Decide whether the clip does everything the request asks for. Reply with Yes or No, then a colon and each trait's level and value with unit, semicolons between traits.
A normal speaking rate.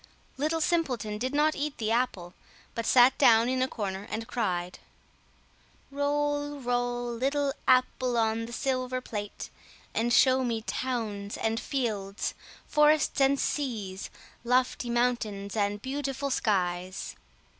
No: slow, 125 wpm